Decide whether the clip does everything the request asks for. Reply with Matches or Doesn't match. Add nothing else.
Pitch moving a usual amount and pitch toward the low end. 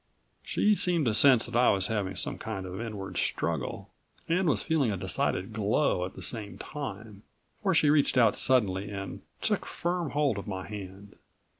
Doesn't match